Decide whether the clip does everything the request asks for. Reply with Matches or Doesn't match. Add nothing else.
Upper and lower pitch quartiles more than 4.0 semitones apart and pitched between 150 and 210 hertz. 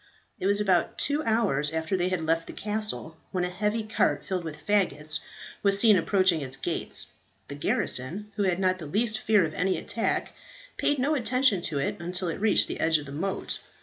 Matches